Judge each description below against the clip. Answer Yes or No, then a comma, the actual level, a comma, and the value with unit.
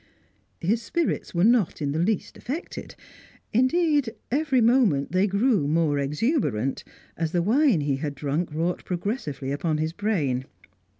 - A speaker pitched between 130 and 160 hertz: No, medium, 180 Hz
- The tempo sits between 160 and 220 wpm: No, average, 140 wpm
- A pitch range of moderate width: No, wide, 8.3 semitones